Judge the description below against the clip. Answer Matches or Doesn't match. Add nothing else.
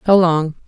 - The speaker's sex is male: Doesn't match